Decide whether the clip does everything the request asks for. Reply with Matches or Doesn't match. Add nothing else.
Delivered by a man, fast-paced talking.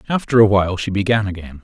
Matches